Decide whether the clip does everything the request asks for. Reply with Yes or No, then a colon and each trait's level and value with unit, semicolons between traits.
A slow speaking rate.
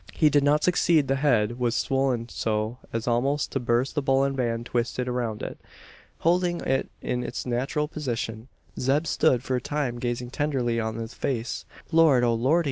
No: average, 180 wpm